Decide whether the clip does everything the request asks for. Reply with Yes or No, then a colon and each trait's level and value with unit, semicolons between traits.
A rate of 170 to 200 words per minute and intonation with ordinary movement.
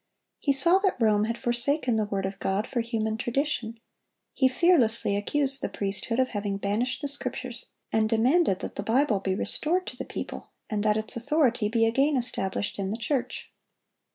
Yes: average, 180 wpm; average, 4.3 semitones